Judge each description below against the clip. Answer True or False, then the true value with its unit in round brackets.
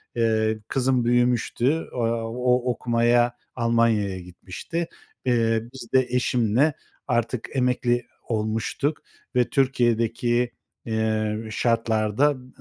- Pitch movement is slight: True (2.0 semitones)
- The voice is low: True (120 Hz)